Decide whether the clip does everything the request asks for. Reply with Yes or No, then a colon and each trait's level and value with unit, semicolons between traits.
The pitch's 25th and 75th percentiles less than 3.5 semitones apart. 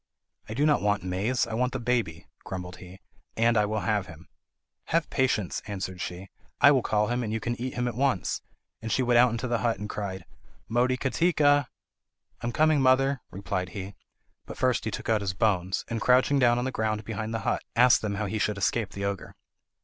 No: average, 4.0 semitones